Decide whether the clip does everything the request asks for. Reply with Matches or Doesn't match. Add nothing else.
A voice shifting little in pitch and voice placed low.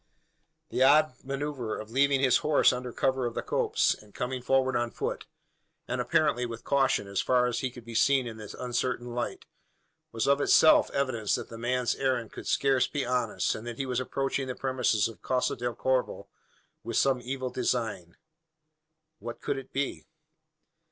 Matches